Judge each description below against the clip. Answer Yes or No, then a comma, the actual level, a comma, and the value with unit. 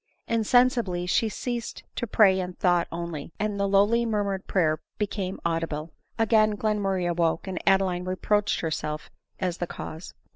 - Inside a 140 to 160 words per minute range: Yes, average, 150 wpm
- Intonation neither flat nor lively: Yes, average, 3.4 semitones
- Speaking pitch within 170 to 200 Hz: Yes, high, 190 Hz